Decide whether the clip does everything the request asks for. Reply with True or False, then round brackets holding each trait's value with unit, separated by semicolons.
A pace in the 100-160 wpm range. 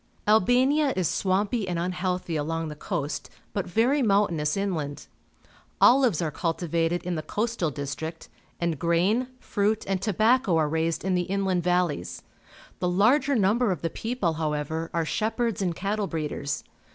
True (150 wpm)